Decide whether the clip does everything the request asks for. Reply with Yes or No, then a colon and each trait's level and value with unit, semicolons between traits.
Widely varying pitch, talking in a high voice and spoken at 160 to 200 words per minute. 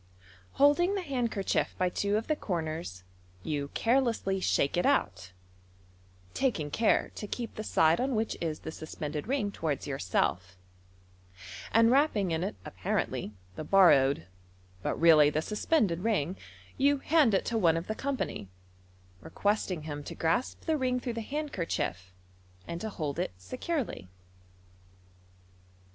No: wide, 8.3 semitones; high, 195 Hz; average, 145 wpm